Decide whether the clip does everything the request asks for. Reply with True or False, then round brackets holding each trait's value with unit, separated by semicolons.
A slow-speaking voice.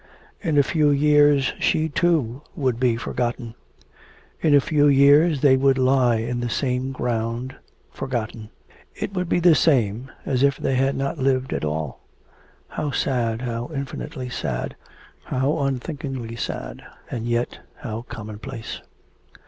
False (145 wpm)